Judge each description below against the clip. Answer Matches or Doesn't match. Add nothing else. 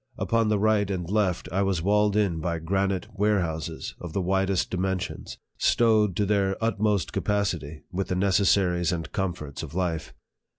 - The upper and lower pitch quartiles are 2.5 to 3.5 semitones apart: Matches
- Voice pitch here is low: Matches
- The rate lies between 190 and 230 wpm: Doesn't match